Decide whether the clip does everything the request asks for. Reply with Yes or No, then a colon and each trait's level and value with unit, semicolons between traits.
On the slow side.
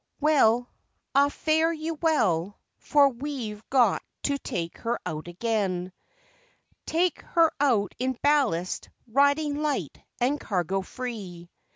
Yes: slow, 115 wpm